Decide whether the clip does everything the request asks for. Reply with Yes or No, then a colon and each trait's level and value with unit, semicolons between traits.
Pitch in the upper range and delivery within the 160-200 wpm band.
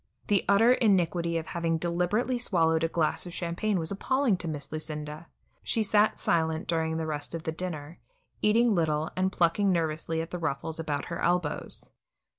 No: medium, 170 Hz; average, 175 wpm